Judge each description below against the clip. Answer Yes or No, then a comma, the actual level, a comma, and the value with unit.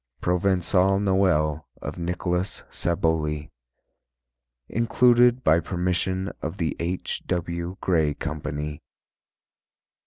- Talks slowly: Yes, slow, 85 wpm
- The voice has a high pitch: No, very low, 90 Hz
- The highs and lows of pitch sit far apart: No, average, 3.0 semitones